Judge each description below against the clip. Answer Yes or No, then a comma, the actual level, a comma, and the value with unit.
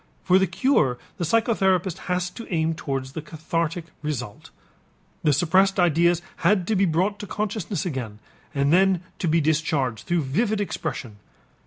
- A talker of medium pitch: Yes, medium, 170 Hz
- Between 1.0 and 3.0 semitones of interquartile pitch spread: No, average, 4.1 semitones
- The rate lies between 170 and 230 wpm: No, average, 155 wpm